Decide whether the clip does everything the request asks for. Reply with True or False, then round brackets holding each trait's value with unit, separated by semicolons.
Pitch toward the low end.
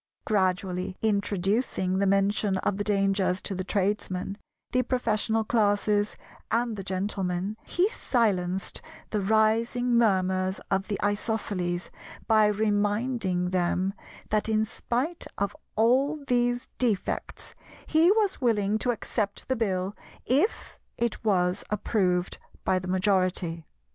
False (205 Hz)